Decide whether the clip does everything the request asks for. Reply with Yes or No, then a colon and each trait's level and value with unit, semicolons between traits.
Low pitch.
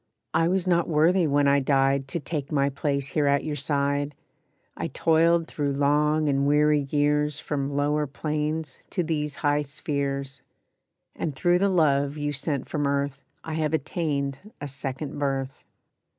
No: medium, 145 Hz